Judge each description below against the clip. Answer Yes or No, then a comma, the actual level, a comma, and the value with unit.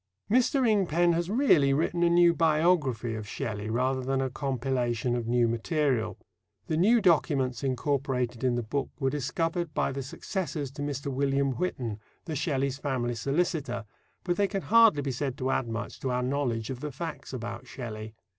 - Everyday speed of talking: Yes, average, 175 wpm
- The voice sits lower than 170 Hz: Yes, low, 135 Hz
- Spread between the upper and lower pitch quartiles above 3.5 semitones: Yes, average, 5.1 semitones